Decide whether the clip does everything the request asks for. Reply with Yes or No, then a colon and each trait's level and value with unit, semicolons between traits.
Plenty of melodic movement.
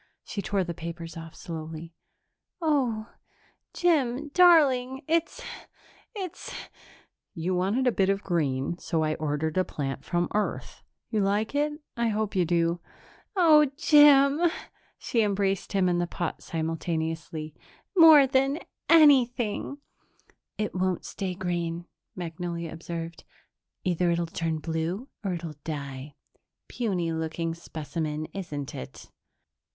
Yes: wide, 6.9 semitones